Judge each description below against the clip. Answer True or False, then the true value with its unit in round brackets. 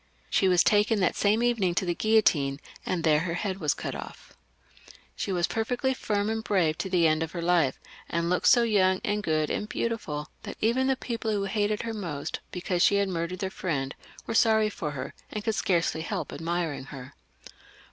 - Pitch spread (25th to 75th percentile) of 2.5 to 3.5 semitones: False (4.5 semitones)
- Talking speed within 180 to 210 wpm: True (200 wpm)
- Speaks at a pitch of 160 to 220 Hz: True (185 Hz)